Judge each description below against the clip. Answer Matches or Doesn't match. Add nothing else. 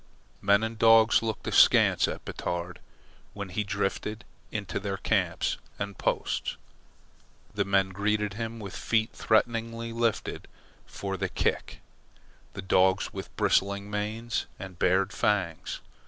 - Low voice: Matches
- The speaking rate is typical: Doesn't match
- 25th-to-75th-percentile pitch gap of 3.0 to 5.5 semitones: Doesn't match